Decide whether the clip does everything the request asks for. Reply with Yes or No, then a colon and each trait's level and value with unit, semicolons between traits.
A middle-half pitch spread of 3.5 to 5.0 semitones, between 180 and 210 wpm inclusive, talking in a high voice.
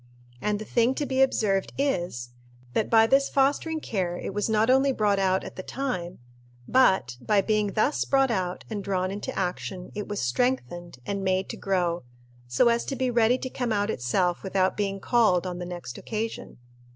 Yes: average, 4.7 semitones; average, 190 wpm; high, 205 Hz